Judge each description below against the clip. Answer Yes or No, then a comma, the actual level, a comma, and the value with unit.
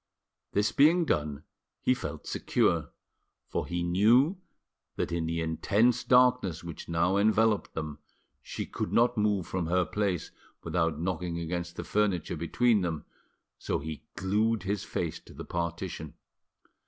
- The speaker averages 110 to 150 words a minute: Yes, average, 140 wpm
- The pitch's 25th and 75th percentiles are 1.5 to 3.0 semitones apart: No, average, 4.6 semitones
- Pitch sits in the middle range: No, very low, 90 Hz